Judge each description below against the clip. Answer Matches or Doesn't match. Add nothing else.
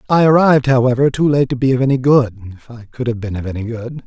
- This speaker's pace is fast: Matches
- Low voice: Matches